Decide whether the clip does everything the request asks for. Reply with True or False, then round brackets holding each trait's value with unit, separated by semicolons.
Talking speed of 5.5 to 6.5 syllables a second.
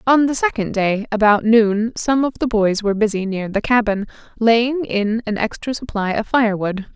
False (4.9 syllables/s)